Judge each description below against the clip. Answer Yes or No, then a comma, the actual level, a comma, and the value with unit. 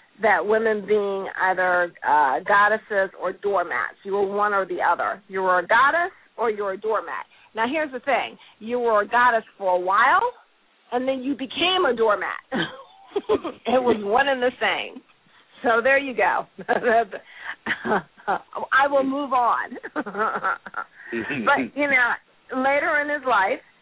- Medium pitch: No, high, 230 Hz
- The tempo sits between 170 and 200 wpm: No, average, 150 wpm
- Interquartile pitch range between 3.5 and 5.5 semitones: Yes, average, 5.2 semitones